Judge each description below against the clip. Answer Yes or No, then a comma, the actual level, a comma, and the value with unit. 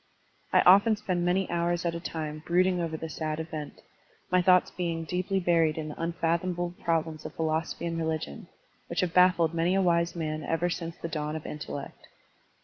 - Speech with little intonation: Yes, narrow, 1.8 semitones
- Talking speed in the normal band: Yes, average, 190 wpm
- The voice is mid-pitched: Yes, medium, 170 Hz